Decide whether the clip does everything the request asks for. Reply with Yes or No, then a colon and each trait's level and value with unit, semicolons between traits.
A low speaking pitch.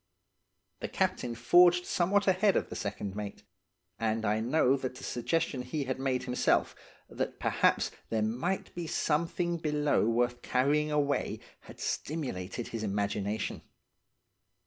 Yes: low, 130 Hz